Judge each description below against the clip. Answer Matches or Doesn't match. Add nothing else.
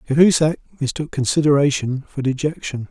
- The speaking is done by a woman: Doesn't match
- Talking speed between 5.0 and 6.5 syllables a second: Matches